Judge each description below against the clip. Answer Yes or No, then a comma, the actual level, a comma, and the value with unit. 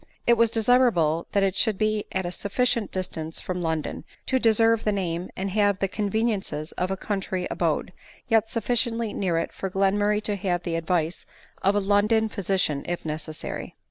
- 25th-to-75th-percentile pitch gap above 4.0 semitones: No, average, 3.7 semitones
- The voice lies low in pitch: No, high, 195 Hz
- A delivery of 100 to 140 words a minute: No, average, 180 wpm